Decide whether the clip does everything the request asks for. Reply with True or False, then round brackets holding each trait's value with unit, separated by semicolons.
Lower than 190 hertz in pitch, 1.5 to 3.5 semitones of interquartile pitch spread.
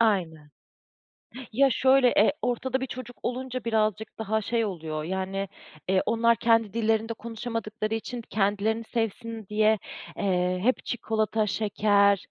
False (220 Hz; 2.4 semitones)